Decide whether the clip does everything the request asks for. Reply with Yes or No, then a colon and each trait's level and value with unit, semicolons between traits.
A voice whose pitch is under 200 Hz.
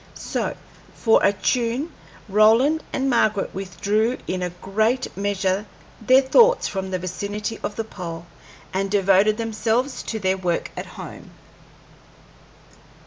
No: high, 210 Hz